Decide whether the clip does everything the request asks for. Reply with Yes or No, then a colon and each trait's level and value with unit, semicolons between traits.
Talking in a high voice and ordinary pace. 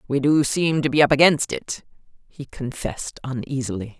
No: medium, 140 Hz; average, 165 wpm